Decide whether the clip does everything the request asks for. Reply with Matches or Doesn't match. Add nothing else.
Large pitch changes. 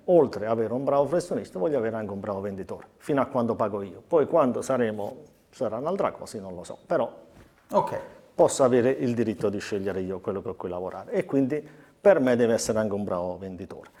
Matches